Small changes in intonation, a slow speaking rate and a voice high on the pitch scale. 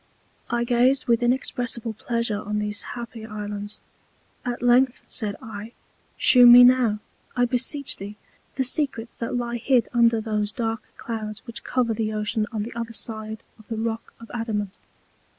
No: narrow, 2.2 semitones; average, 160 wpm; high, 230 Hz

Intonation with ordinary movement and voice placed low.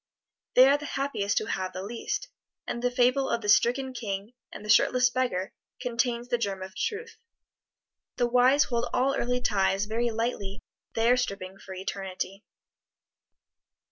No: average, 4.0 semitones; high, 235 Hz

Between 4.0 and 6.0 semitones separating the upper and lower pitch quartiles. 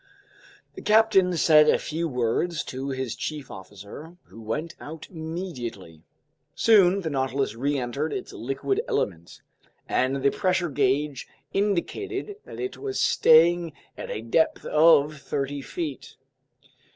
Yes: average, 4.9 semitones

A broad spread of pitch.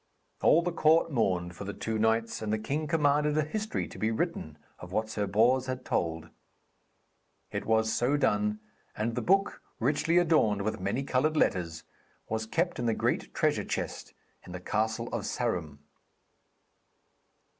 Yes: wide, 6.3 semitones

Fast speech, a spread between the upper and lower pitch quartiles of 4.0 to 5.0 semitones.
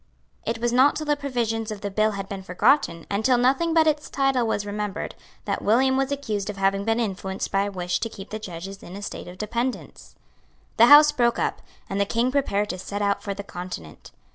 Yes: fast, 225 wpm; average, 4.6 semitones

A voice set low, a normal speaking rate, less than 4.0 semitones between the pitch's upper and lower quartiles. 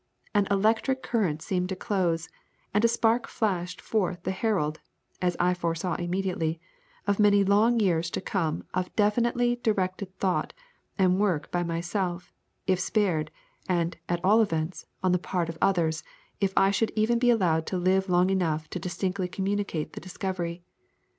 No: medium, 185 Hz; average, 160 wpm; average, 2.9 semitones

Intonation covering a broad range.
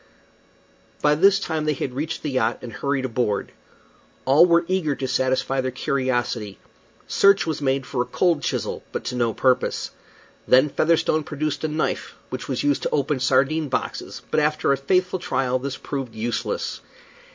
No: average, 3.2 semitones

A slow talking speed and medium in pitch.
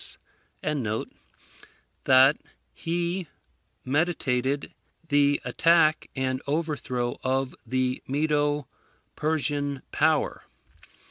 Yes: slow, 70 wpm; medium, 145 Hz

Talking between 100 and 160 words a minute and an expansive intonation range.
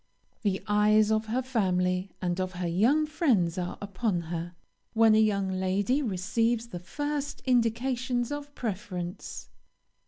No: slow, 135 wpm; average, 4.8 semitones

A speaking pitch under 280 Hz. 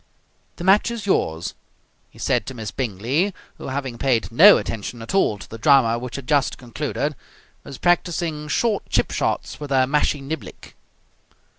Yes: medium, 140 Hz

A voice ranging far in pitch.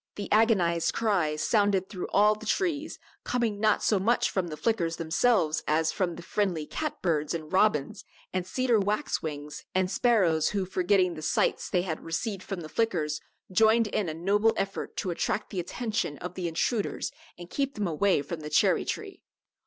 No: average, 4.5 semitones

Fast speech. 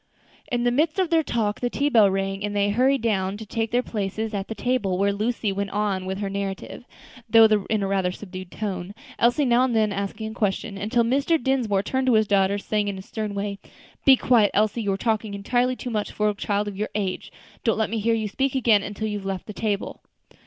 Yes: fast, 240 wpm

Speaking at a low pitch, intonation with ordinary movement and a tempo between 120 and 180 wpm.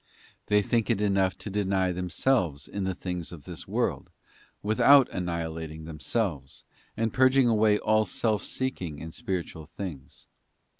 Yes: very low, 95 Hz; average, 4.9 semitones; average, 140 wpm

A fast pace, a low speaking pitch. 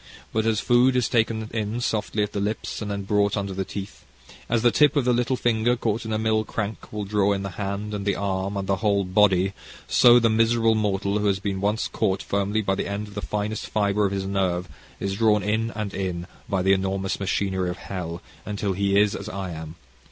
Yes: fast, 230 wpm; low, 100 Hz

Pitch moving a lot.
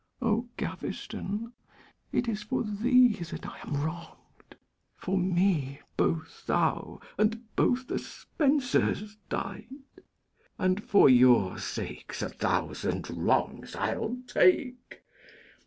Yes: wide, 5.8 semitones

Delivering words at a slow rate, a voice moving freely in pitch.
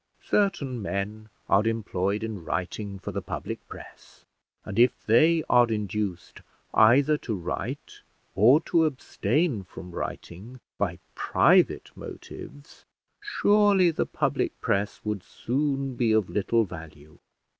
Yes: slow, 125 wpm; wide, 6.0 semitones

